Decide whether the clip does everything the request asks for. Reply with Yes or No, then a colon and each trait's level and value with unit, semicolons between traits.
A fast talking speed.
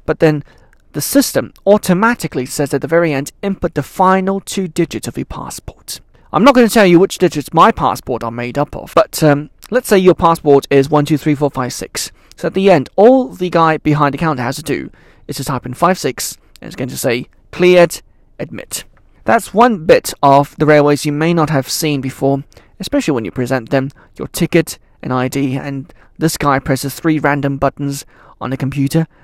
Yes: fast, 210 wpm